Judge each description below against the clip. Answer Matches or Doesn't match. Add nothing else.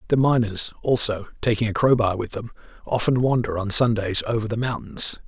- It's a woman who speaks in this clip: Doesn't match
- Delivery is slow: Doesn't match